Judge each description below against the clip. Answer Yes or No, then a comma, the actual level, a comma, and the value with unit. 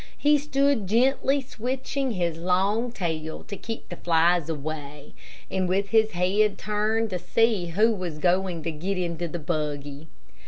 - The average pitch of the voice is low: No, medium, 185 Hz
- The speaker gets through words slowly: No, average, 155 wpm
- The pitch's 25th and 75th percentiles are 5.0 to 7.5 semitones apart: Yes, average, 5.3 semitones